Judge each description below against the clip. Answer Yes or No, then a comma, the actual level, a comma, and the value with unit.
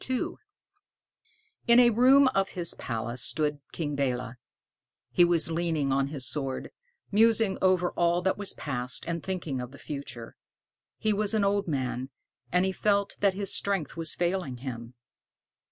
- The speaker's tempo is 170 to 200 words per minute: No, average, 155 wpm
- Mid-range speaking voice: Yes, medium, 170 Hz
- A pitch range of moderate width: No, wide, 6.6 semitones